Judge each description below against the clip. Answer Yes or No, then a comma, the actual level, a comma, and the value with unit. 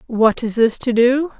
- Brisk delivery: Yes, fast, 215 wpm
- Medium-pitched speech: No, high, 240 Hz